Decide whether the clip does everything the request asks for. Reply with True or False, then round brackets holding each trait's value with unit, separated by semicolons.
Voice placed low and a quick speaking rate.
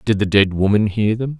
True (105 Hz; 260 wpm)